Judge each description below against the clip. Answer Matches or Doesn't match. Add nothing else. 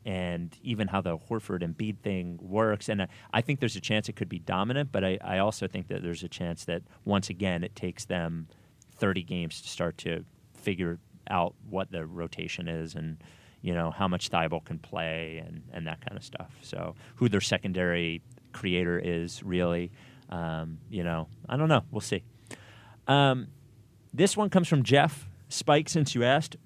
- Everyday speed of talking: Matches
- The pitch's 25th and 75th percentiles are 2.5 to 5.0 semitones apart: Doesn't match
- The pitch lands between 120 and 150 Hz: Doesn't match